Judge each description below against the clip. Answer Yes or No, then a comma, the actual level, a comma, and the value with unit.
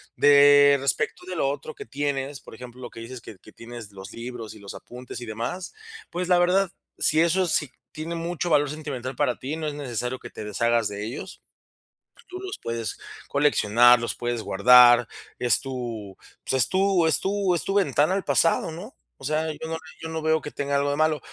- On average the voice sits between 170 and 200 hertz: No, medium, 140 Hz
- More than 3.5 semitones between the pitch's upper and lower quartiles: Yes, average, 5.1 semitones